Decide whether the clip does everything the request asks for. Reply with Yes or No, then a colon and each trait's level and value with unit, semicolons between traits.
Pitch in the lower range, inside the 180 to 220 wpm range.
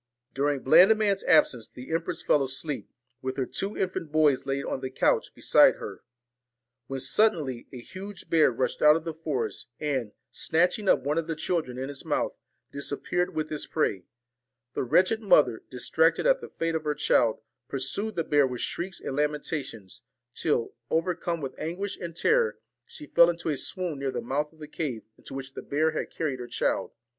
No: medium, 150 Hz; average, 190 wpm